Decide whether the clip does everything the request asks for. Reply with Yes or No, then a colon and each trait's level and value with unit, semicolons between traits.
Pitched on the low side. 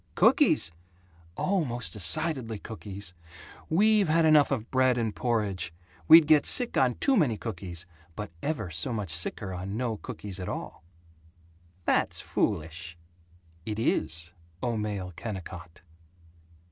Yes: low, 110 Hz